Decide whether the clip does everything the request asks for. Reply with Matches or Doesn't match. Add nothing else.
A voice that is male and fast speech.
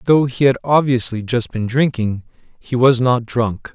Doesn't match